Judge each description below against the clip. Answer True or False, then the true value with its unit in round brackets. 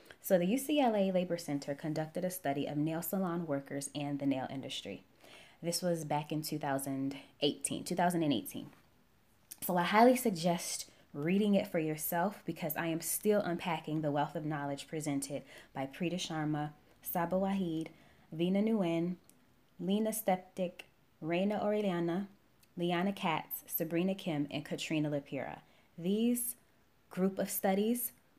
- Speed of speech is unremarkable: False (130 wpm)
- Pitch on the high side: False (170 Hz)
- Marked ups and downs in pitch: False (4.3 semitones)